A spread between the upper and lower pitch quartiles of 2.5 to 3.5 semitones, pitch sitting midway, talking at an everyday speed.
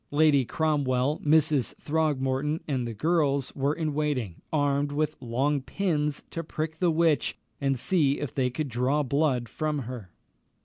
Yes: average, 2.8 semitones; medium, 145 Hz; average, 150 wpm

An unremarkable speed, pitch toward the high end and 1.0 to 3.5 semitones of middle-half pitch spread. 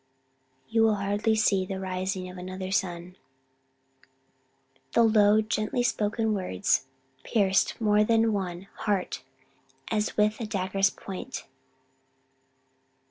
No: slow, 110 wpm; high, 205 Hz; narrow, 2.5 semitones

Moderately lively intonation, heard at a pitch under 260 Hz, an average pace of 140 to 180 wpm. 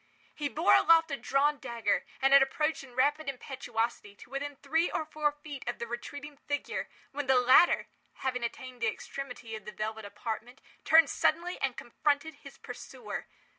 No: average, 3.6 semitones; very high, 275 Hz; average, 170 wpm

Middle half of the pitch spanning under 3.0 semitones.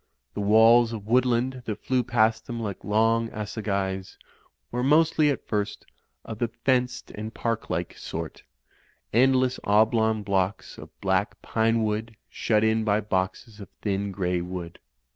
Yes: narrow, 2.6 semitones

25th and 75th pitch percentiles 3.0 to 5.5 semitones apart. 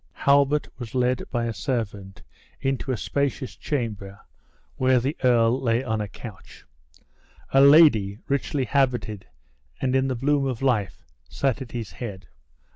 Yes: average, 3.6 semitones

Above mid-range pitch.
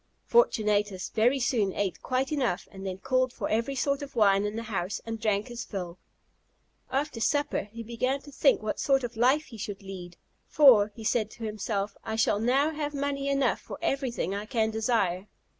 Yes: high, 230 Hz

